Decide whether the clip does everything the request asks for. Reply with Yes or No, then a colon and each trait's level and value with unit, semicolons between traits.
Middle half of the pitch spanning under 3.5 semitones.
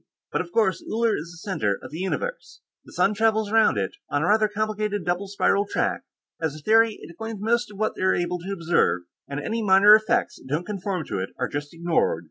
No: average, 4.4 semitones